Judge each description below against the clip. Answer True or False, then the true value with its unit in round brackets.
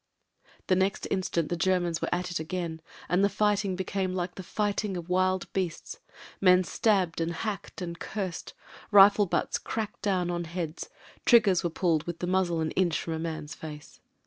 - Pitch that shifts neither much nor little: False (2.3 semitones)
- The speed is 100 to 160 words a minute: False (180 wpm)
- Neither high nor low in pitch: True (180 Hz)